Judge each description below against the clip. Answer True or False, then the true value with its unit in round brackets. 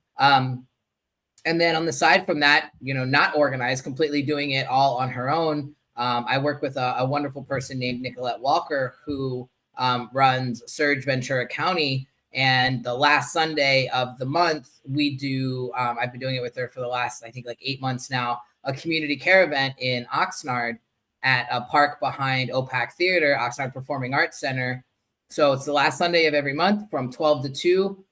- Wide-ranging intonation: False (2.7 semitones)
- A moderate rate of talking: True (190 wpm)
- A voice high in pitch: False (135 Hz)